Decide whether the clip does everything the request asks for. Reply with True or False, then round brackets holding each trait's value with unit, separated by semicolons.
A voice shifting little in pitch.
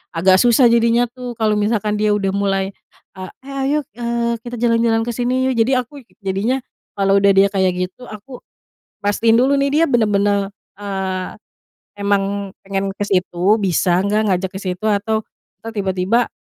False (3.4 semitones)